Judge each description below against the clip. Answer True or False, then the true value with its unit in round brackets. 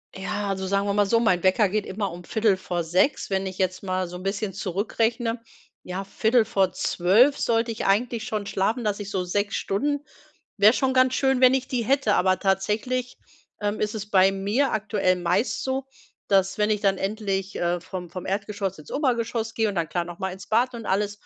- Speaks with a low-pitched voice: False (205 Hz)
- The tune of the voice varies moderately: True (3.1 semitones)